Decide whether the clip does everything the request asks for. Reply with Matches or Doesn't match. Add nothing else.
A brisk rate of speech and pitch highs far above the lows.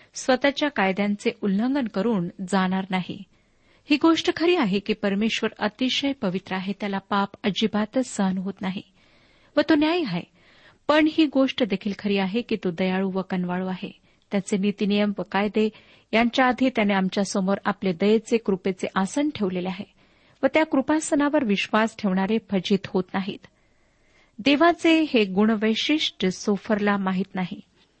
Doesn't match